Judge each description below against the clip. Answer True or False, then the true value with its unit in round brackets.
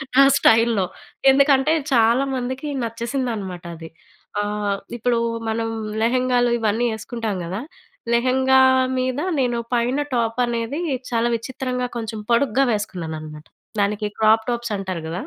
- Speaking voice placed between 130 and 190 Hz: False (235 Hz)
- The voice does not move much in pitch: False (3.2 semitones)